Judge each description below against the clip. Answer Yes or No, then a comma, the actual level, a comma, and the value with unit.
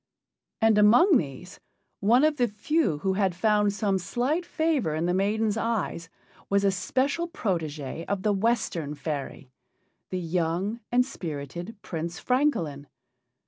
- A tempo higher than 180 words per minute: No, average, 140 wpm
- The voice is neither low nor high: No, high, 200 Hz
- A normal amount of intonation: No, wide, 6.1 semitones